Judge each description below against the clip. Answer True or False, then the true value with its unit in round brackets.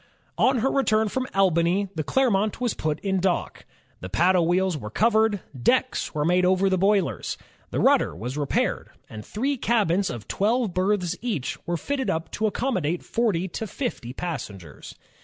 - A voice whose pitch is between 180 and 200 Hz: True (190 Hz)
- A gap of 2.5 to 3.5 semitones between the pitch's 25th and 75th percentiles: False (5.0 semitones)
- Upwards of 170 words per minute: False (165 wpm)